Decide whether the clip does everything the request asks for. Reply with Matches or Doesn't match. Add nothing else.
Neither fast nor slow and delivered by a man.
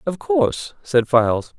Matches